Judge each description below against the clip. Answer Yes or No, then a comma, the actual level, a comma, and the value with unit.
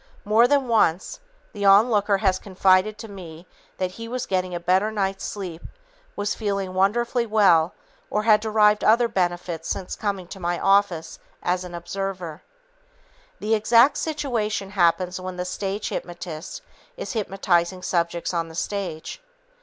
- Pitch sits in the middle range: No, high, 195 Hz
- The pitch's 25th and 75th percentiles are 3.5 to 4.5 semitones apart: No, average, 3.0 semitones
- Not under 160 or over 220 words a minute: No, average, 145 wpm